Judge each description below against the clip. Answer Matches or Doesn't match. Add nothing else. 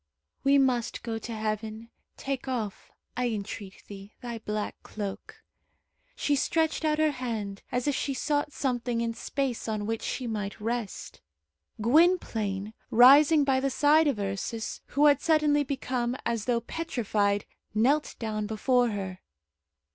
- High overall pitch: Matches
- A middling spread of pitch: Matches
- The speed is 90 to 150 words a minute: Matches